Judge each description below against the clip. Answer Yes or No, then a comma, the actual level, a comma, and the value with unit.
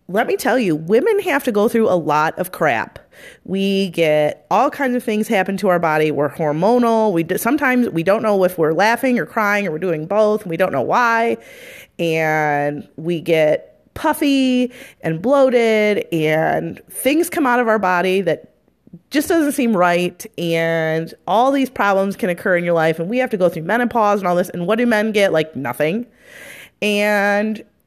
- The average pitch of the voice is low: No, high, 205 Hz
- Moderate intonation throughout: No, wide, 6.3 semitones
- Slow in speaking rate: No, average, 195 wpm